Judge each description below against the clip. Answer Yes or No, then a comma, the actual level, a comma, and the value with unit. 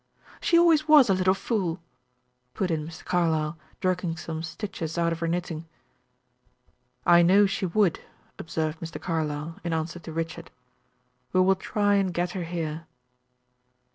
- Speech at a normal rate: Yes, average, 150 wpm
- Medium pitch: Yes, medium, 170 Hz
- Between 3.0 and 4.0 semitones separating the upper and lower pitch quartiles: No, narrow, 2.4 semitones